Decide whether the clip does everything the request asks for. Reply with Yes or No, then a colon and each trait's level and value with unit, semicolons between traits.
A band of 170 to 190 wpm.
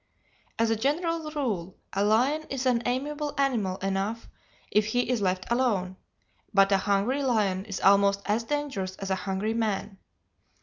No: average, 160 wpm